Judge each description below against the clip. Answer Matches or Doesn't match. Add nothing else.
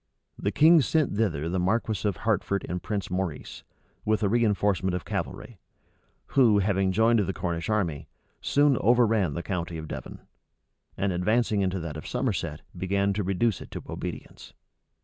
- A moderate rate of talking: Matches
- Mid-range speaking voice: Doesn't match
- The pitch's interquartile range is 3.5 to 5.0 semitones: Matches